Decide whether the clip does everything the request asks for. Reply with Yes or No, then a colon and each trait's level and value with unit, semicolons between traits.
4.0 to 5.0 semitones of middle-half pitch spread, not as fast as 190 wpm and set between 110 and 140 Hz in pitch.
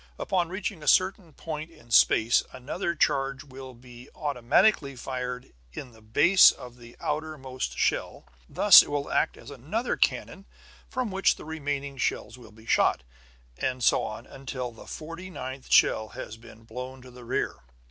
Yes: average, 4.3 semitones; average, 165 wpm; low, 135 Hz